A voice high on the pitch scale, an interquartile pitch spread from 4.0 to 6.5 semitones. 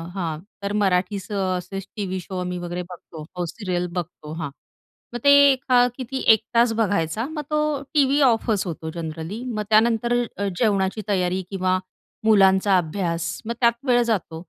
Yes: high, 195 Hz; average, 4.4 semitones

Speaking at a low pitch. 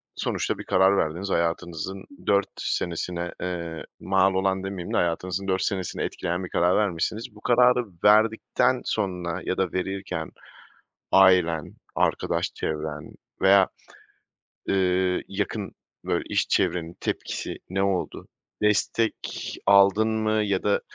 Yes: very low, 95 Hz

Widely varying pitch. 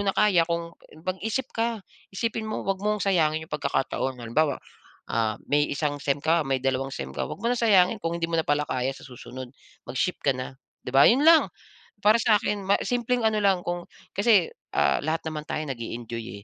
Yes: wide, 7.5 semitones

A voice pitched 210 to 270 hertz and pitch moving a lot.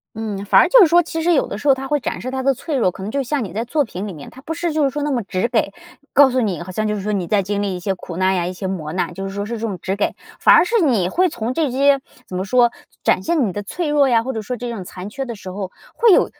Yes: high, 230 Hz; wide, 6.4 semitones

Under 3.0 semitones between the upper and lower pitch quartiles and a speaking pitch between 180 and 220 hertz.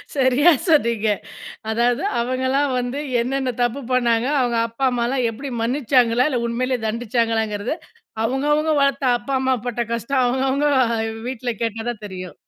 No: narrow, 2.5 semitones; high, 245 Hz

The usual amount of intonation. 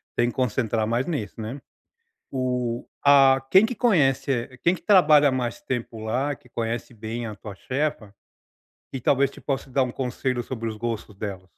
Yes: average, 3.3 semitones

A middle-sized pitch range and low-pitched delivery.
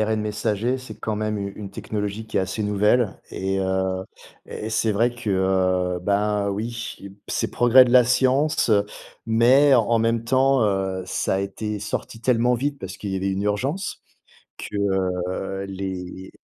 Yes: average, 3.4 semitones; low, 105 Hz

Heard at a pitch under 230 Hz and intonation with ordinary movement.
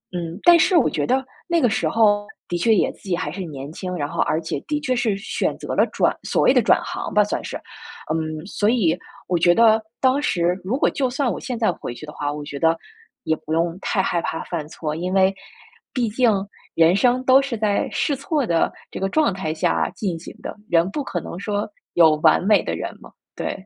No: high, 190 Hz; wide, 6.3 semitones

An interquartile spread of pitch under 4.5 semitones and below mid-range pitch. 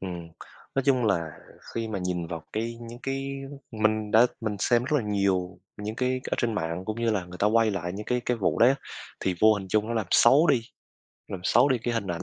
Yes: average, 3.8 semitones; low, 110 Hz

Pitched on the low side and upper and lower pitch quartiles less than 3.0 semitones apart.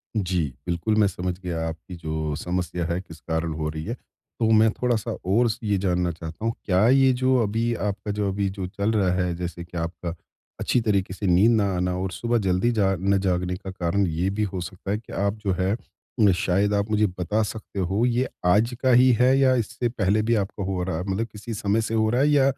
No: low, 100 Hz; average, 3.7 semitones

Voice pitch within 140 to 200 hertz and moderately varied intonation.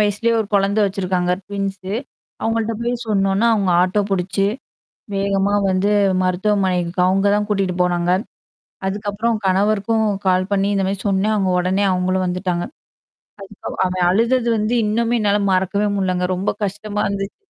No: high, 195 Hz; narrow, 2.1 semitones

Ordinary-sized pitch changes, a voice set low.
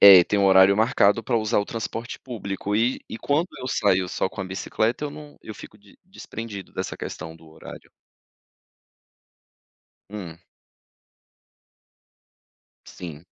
Yes: average, 3.6 semitones; low, 105 Hz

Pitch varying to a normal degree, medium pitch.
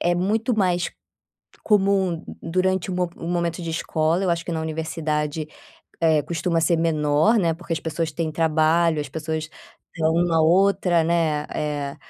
No: narrow, 2.0 semitones; medium, 165 Hz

